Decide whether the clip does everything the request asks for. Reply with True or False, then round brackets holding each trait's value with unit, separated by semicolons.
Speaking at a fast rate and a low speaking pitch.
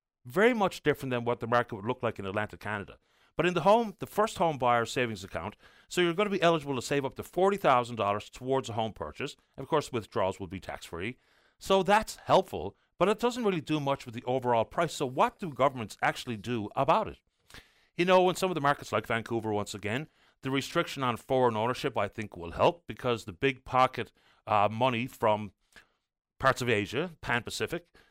True (210 wpm; 125 Hz)